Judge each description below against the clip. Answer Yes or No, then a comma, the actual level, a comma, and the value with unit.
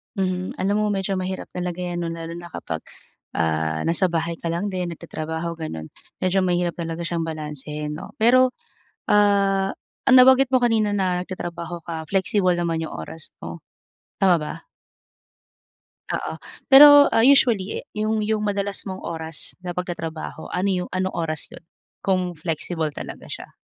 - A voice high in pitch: No, medium, 180 Hz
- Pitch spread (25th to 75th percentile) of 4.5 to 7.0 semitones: No, average, 3.5 semitones